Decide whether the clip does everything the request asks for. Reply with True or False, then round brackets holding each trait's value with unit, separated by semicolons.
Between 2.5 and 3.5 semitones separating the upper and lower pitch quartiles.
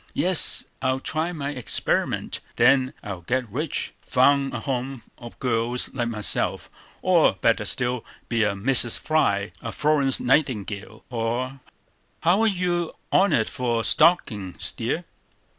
False (4.5 semitones)